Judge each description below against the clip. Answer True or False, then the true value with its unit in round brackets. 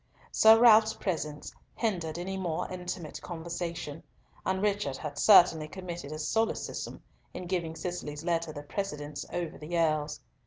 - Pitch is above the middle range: False (170 Hz)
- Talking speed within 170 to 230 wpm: False (140 wpm)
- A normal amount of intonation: True (3.5 semitones)